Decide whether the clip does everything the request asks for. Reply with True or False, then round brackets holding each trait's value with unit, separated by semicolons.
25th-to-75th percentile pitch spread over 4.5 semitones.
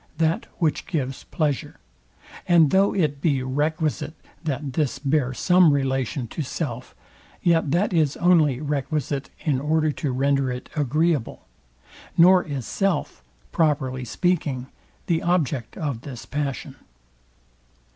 False (3.4 semitones)